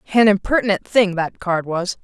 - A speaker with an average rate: Yes, average, 175 wpm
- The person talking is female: Yes, female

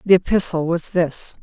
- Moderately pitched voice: Yes, medium, 170 Hz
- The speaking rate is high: No, average, 170 wpm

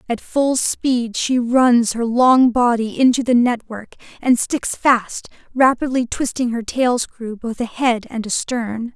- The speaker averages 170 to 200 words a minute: No, average, 155 wpm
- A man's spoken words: No, female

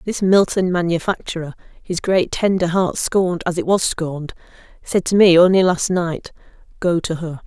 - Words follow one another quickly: No, average, 170 wpm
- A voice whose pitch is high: No, medium, 175 Hz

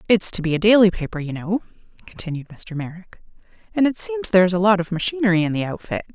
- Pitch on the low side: No, high, 190 Hz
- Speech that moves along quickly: Yes, fast, 215 wpm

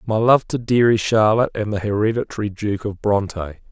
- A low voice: Yes, low, 105 Hz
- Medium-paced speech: Yes, average, 180 wpm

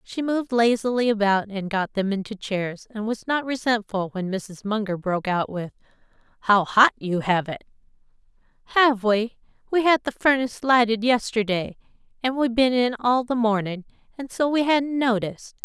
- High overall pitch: Yes, high, 225 Hz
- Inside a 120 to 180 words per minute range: Yes, average, 170 wpm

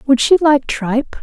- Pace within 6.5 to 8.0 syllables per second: No, 4.8 syllables/s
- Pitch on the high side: Yes, very high, 265 Hz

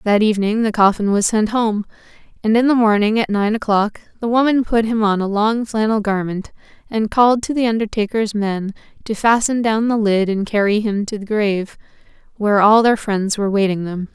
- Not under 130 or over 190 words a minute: No, average, 200 wpm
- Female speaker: Yes, female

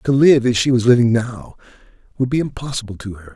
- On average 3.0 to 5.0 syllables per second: No, 6.1 syllables/s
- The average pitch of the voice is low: Yes, low, 125 Hz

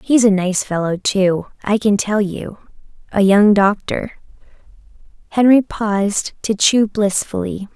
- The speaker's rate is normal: No, slow, 125 wpm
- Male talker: No, female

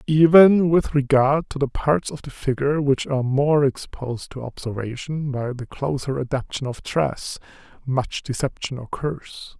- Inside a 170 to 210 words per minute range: No, average, 150 wpm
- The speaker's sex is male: Yes, male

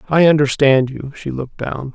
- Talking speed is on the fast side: No, average, 185 wpm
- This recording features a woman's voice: No, male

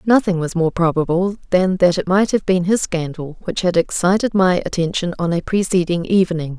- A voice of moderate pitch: Yes, medium, 180 Hz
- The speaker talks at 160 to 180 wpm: No, average, 190 wpm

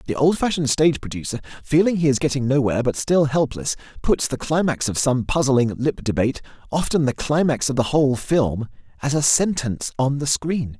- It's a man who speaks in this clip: Yes, male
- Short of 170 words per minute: No, average, 185 wpm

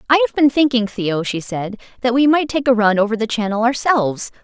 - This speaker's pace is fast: Yes, fast, 230 wpm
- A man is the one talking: No, female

